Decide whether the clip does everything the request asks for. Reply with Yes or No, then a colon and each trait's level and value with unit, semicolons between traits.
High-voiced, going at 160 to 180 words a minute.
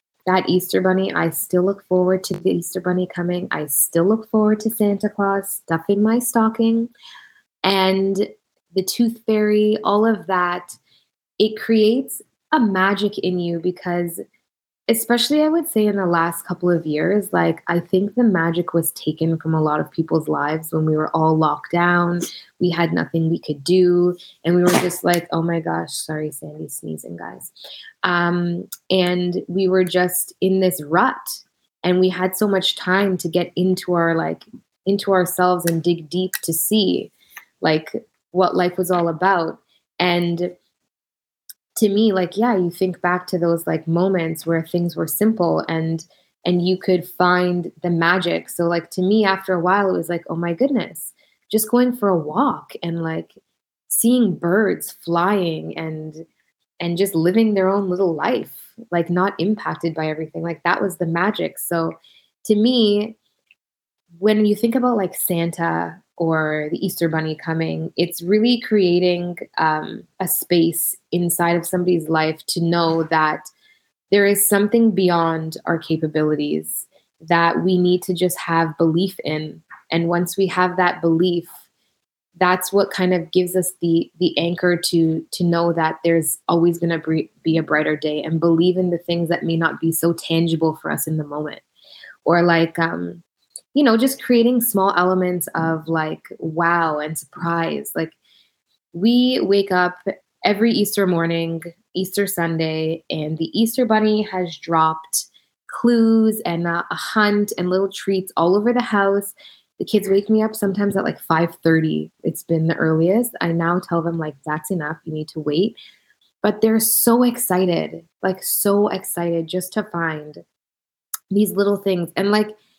No: medium, 180 Hz; average, 170 wpm